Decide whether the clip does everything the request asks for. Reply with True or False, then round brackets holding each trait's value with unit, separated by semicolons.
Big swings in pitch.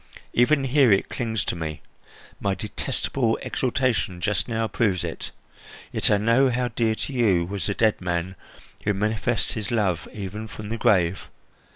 False (3.7 semitones)